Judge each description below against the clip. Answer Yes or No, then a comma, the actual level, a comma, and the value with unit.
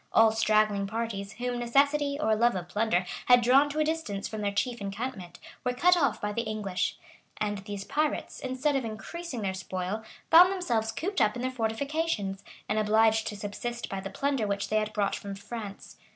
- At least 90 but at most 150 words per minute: No, average, 195 wpm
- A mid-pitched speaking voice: No, high, 220 Hz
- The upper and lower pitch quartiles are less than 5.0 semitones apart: Yes, average, 4.2 semitones